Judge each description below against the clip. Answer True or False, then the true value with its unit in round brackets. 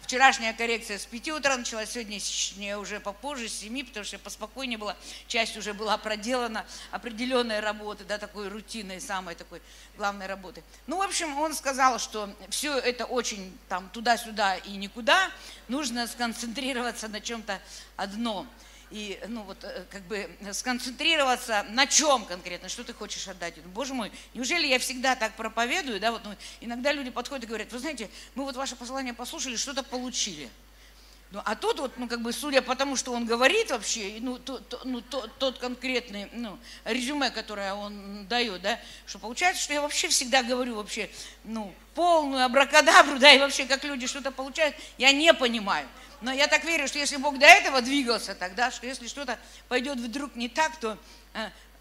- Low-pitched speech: False (240 Hz)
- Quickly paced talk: True (175 wpm)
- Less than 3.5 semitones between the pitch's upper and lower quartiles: False (4.2 semitones)